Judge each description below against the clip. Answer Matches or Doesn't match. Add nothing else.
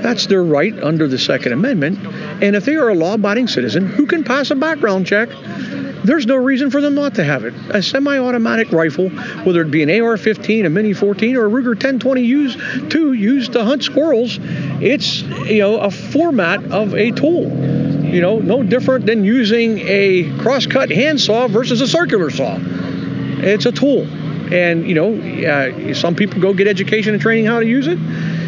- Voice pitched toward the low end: Doesn't match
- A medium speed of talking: Matches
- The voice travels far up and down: Matches